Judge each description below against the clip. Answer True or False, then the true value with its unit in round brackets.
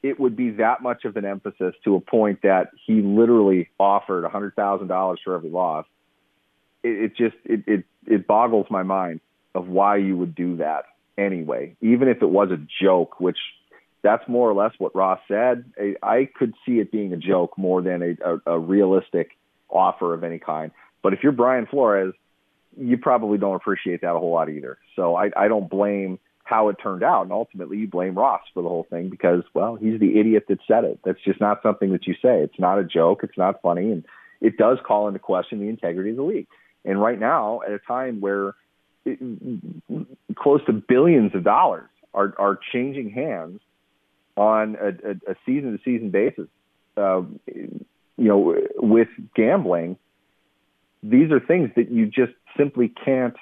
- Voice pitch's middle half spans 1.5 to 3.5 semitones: False (4.2 semitones)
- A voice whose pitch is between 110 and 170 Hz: False (100 Hz)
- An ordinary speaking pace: True (190 wpm)